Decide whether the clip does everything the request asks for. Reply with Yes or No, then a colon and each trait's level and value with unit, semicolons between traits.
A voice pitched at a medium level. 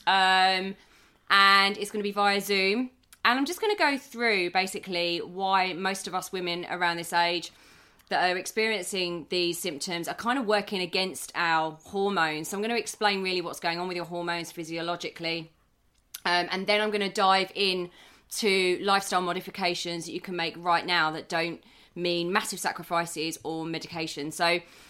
Yes: medium, 180 Hz